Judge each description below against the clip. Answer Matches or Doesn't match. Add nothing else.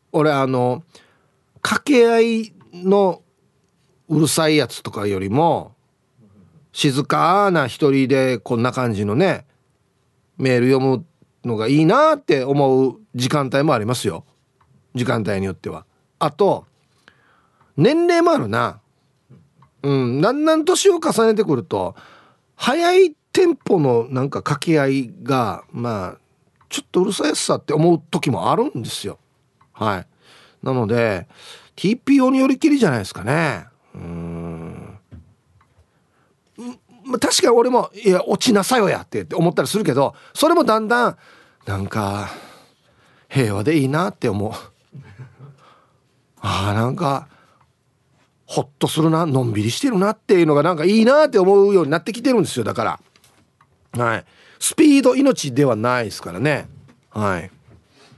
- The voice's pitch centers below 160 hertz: Matches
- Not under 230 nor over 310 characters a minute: Matches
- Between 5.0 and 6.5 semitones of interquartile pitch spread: Doesn't match